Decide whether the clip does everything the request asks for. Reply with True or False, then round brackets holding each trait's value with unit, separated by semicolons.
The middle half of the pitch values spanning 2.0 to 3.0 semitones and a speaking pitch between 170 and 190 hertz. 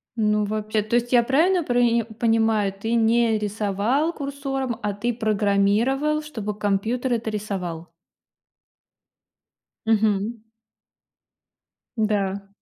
False (2.7 semitones; 220 Hz)